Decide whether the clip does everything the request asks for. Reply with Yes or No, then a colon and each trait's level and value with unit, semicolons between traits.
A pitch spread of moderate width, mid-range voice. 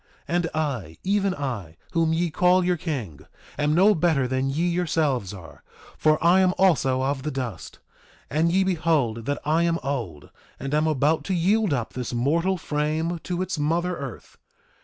Yes: average, 4.8 semitones; medium, 155 Hz